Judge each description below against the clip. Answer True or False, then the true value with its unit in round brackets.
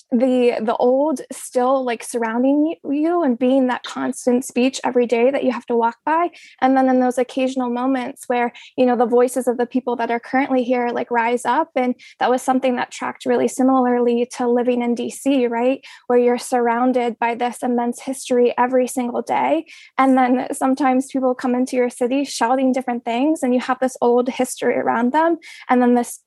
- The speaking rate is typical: True (195 wpm)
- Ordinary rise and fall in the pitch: False (1.4 semitones)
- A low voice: False (255 Hz)